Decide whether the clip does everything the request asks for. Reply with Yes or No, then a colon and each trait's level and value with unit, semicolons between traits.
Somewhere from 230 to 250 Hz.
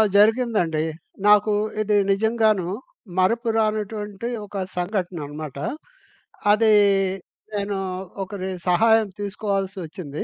No: high, 205 Hz